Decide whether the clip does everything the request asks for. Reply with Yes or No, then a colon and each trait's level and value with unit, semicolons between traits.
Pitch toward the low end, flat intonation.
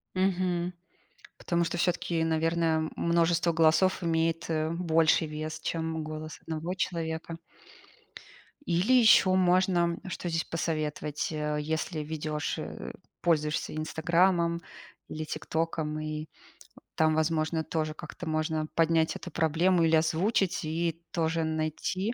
No: medium, 165 Hz; narrow, 1.6 semitones